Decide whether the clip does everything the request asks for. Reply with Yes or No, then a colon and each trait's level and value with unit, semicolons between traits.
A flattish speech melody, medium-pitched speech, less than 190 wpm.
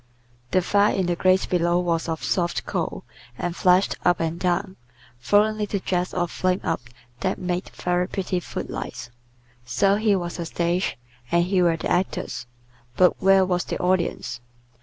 Yes: narrow, 1.6 semitones; medium, 180 Hz; average, 170 wpm